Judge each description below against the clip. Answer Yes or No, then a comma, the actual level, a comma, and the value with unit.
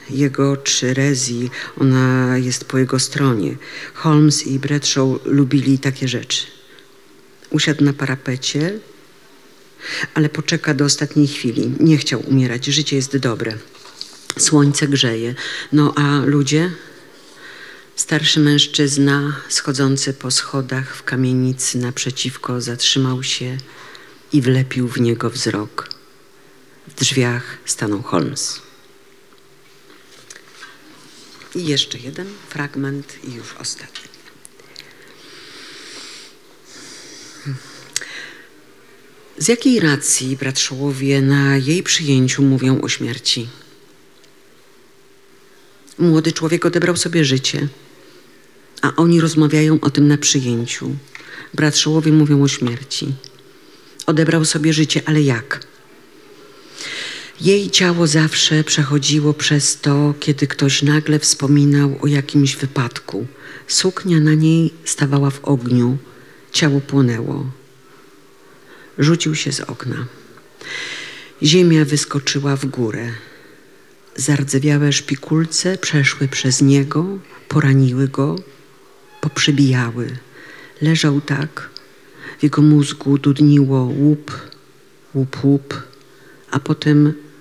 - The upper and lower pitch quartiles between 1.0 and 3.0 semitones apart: Yes, average, 2.7 semitones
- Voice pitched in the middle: Yes, medium, 145 Hz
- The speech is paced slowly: Yes, slow, 95 wpm